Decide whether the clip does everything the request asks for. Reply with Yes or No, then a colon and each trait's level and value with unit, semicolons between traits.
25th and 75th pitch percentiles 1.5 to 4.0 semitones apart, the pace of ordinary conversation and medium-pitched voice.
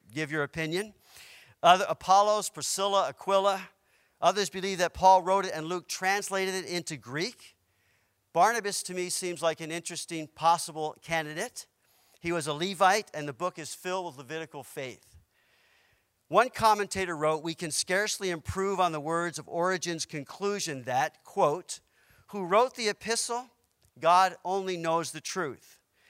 Yes: average, 3.2 semitones; average, 145 wpm; medium, 180 Hz